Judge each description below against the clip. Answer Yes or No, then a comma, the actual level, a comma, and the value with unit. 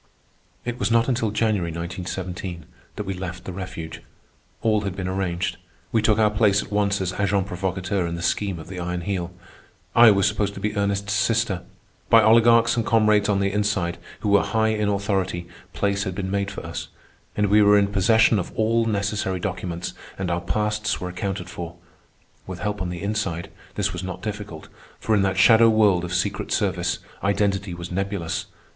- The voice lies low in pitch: Yes, low, 100 Hz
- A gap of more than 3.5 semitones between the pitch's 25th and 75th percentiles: No, narrow, 2.6 semitones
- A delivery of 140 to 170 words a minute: No, average, 190 wpm